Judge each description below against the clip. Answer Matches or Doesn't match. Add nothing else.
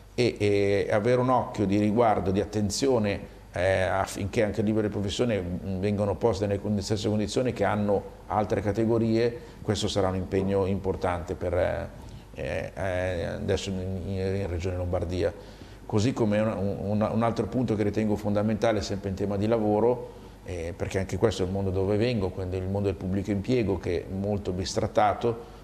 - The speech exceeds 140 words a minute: Matches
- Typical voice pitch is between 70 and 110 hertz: Matches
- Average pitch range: Doesn't match